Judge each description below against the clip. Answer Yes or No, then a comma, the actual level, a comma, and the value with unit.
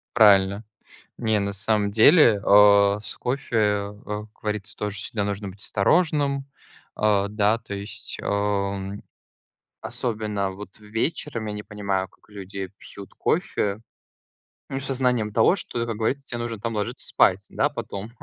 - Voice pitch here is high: No, low, 105 Hz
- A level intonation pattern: Yes, narrow, 2.3 semitones